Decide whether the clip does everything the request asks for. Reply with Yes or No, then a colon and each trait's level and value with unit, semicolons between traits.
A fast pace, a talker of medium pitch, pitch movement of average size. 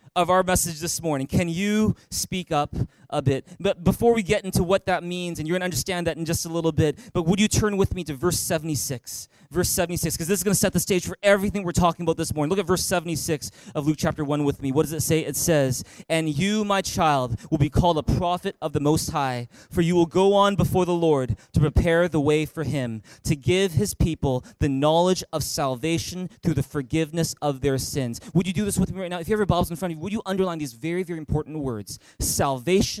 Yes: fast, 255 wpm; medium, 165 Hz; average, 3.6 semitones